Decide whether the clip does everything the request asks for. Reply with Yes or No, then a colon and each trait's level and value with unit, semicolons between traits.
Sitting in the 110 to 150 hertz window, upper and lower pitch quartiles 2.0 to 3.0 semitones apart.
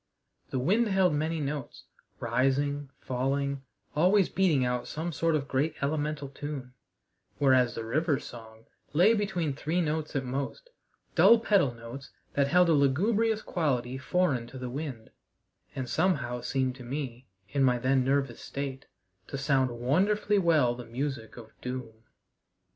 No: medium, 140 Hz; average, 4.1 semitones